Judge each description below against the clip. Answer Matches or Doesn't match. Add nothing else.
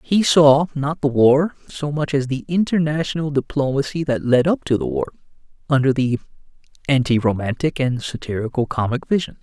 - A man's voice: Matches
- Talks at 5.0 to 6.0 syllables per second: Matches